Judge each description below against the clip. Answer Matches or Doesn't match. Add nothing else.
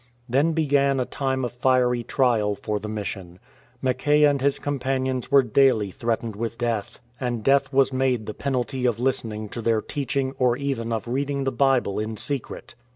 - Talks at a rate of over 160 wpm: Matches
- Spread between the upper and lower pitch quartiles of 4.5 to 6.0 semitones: Doesn't match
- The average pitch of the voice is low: Matches